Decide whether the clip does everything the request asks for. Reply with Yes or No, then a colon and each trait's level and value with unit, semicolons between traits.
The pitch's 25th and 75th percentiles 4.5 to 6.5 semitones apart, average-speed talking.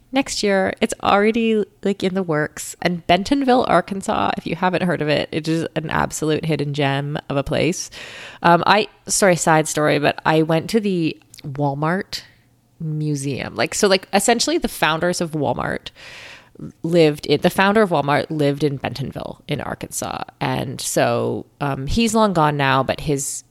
Yes: average, 5.2 semitones; average, 170 wpm